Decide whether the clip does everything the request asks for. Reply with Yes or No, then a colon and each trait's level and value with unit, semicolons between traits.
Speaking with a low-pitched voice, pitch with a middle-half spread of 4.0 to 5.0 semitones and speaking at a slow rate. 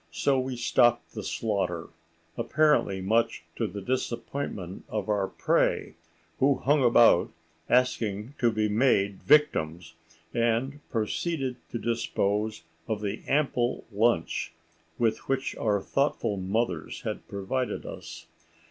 Yes: low, 110 Hz; average, 4.7 semitones; slow, 110 wpm